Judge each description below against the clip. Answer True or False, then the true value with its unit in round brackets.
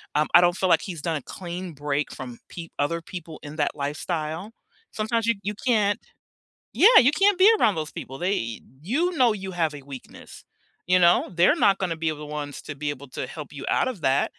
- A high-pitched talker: False (170 Hz)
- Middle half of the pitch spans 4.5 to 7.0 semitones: True (5.3 semitones)